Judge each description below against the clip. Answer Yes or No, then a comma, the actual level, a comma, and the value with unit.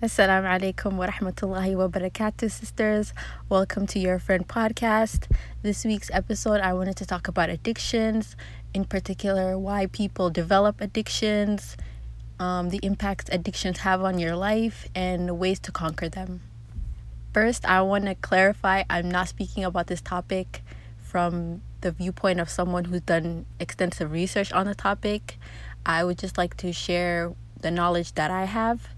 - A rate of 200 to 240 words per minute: No, average, 155 wpm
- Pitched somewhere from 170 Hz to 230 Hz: Yes, high, 190 Hz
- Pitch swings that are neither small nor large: No, narrow, 2.3 semitones